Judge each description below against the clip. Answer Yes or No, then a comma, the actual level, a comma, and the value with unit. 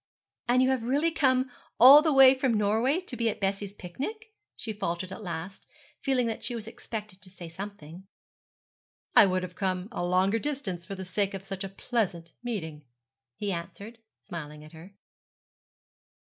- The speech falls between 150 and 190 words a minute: Yes, average, 175 wpm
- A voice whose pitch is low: No, high, 200 Hz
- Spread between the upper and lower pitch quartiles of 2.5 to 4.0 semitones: No, average, 5.1 semitones